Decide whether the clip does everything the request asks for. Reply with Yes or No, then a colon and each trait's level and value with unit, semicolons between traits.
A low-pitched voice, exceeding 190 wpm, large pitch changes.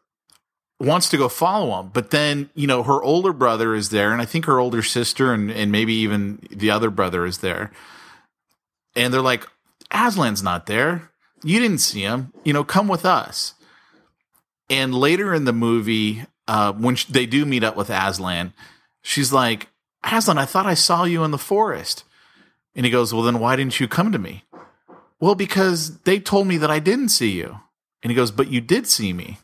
Yes: low, 125 Hz; average, 200 wpm; wide, 6.8 semitones